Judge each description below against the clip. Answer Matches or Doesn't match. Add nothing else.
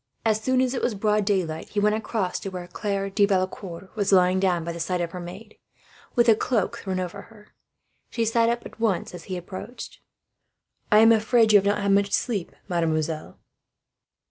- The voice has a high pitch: Matches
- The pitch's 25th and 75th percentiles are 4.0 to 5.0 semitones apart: Doesn't match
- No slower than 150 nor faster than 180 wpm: Doesn't match